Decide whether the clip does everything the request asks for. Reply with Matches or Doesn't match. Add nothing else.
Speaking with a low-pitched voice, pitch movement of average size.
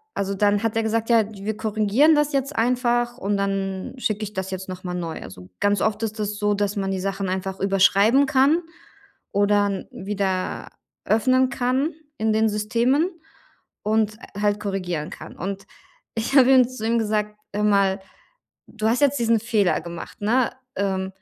Doesn't match